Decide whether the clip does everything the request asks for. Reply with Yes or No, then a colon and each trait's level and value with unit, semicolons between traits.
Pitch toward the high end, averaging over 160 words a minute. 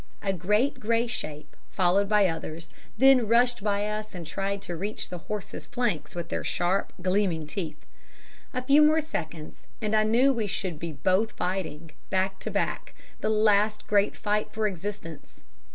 Yes: high, 200 Hz; average, 170 wpm